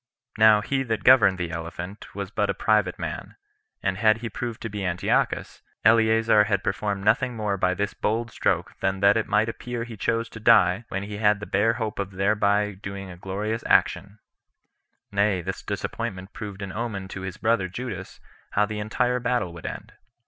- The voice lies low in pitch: Yes, low, 105 Hz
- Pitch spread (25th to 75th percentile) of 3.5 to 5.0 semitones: No, narrow, 2.6 semitones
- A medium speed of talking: Yes, average, 190 wpm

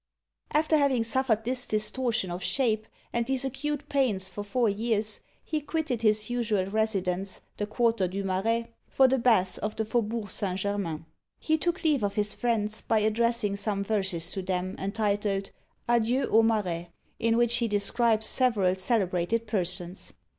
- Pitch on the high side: Yes, high, 215 Hz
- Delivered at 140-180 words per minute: Yes, average, 160 wpm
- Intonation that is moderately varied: Yes, average, 3.4 semitones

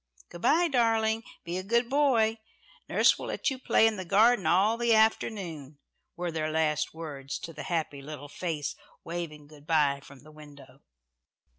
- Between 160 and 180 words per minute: Yes, average, 170 wpm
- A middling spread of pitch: No, wide, 6.6 semitones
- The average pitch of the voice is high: No, medium, 170 Hz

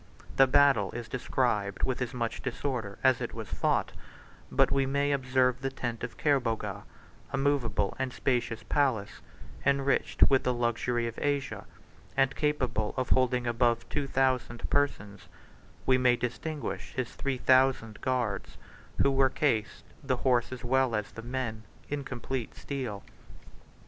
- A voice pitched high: No, low, 125 Hz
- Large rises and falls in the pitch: No, narrow, 2.4 semitones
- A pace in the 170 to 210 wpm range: No, average, 150 wpm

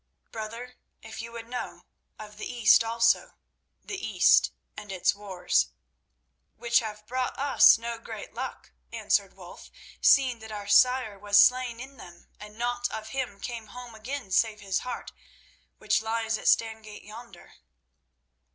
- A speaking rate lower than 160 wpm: Yes, average, 145 wpm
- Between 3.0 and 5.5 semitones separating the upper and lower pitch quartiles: No, narrow, 2.5 semitones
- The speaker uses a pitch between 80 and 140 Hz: No, high, 225 Hz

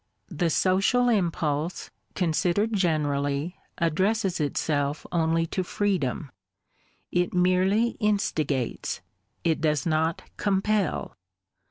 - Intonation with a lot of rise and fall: No, average, 4.1 semitones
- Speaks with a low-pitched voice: No, medium, 170 Hz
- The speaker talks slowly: Yes, slow, 90 wpm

